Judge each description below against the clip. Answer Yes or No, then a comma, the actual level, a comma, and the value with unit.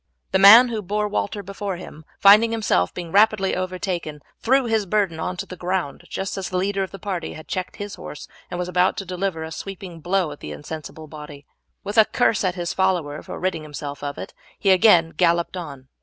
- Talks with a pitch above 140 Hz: Yes, medium, 185 Hz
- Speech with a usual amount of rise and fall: Yes, average, 3.6 semitones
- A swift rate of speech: Yes, fast, 215 wpm